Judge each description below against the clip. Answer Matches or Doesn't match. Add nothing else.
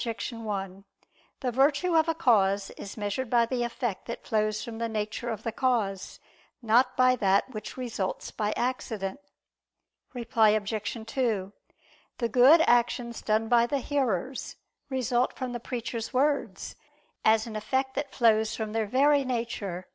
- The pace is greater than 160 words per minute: Doesn't match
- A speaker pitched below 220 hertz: Doesn't match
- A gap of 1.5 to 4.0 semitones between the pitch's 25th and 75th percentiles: Matches